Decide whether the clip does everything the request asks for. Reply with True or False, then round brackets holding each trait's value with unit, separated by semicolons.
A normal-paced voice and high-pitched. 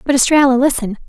True (165 wpm; 260 Hz)